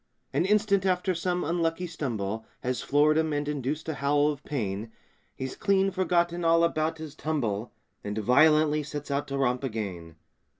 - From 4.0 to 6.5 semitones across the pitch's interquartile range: Yes, average, 4.6 semitones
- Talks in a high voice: No, medium, 150 Hz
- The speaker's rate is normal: Yes, average, 165 wpm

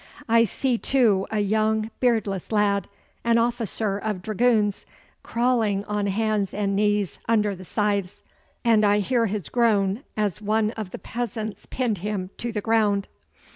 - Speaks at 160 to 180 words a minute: No, average, 150 wpm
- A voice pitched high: Yes, high, 210 Hz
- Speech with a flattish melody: Yes, narrow, 2.1 semitones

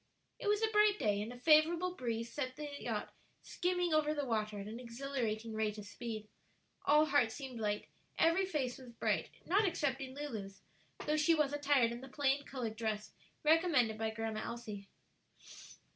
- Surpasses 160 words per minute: Yes, average, 175 wpm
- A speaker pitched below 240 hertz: No, very high, 260 Hz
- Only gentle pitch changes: No, wide, 5.5 semitones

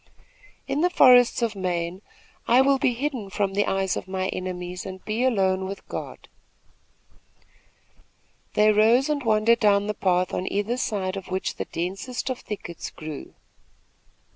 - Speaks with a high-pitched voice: Yes, high, 205 Hz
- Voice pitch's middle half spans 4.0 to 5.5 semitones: Yes, average, 4.4 semitones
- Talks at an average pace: Yes, average, 155 wpm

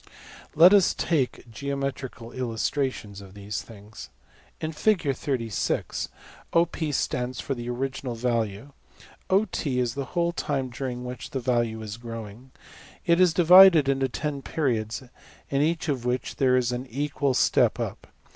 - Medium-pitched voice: No, low, 130 Hz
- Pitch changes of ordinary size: Yes, average, 3.8 semitones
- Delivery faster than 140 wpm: No, slow, 135 wpm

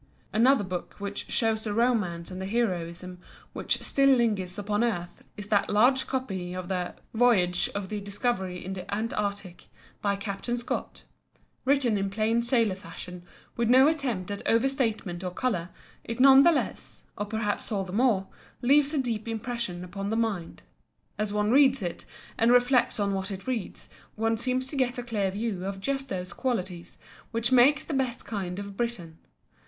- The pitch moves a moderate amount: Yes, average, 4.3 semitones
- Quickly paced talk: No, average, 175 wpm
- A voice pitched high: Yes, high, 215 Hz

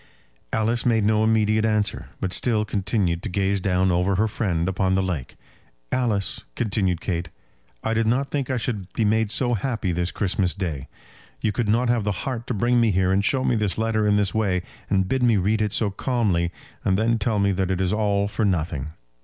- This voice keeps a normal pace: No, fast, 210 wpm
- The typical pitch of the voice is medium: No, low, 105 Hz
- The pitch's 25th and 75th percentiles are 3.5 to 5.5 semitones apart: No, average, 3.0 semitones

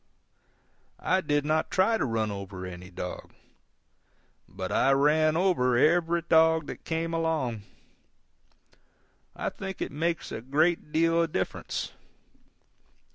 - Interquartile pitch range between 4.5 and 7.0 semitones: Yes, wide, 5.6 semitones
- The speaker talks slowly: Yes, slow, 125 wpm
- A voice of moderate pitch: Yes, medium, 155 Hz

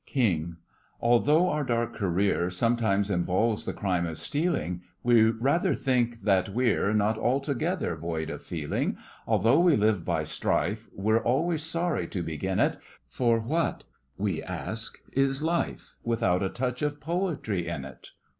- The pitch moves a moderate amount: No, wide, 6.4 semitones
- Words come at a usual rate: Yes, average, 145 wpm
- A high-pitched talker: No, low, 115 Hz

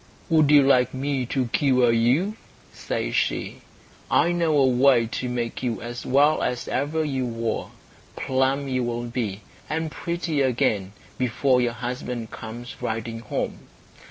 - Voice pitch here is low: Yes, low, 125 Hz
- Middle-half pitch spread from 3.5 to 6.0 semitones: No, average, 3.0 semitones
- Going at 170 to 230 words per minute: No, average, 150 wpm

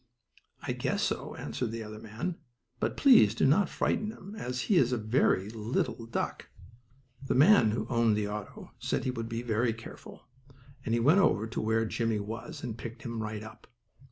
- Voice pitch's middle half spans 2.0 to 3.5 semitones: Yes, average, 2.9 semitones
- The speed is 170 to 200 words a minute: Yes, average, 180 wpm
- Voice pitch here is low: Yes, low, 115 Hz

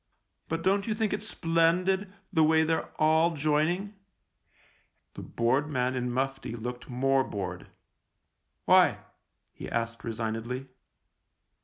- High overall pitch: No, medium, 150 Hz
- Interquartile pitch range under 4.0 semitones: No, average, 5.1 semitones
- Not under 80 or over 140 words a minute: Yes, slow, 135 wpm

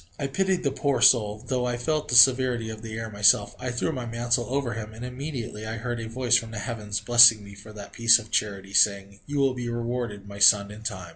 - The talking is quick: Yes, fast, 240 wpm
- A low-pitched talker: Yes, low, 115 Hz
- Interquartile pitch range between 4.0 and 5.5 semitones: No, average, 2.9 semitones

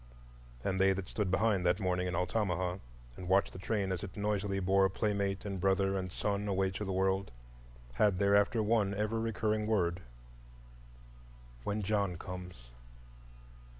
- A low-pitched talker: Yes, very low, 95 Hz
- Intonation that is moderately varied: No, narrow, 2.3 semitones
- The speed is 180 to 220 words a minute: No, average, 150 wpm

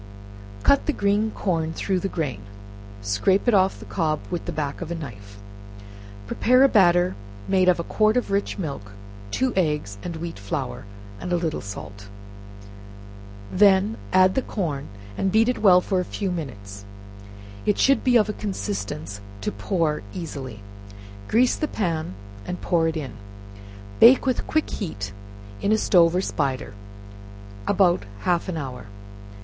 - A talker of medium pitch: Yes, medium, 175 Hz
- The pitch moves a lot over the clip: Yes, wide, 6.1 semitones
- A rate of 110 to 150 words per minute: No, average, 160 wpm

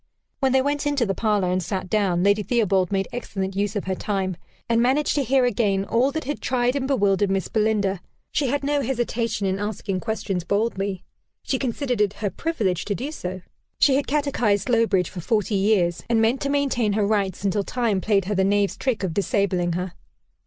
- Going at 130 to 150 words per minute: No, average, 200 wpm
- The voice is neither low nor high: No, high, 210 Hz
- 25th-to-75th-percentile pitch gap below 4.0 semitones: No, average, 4.3 semitones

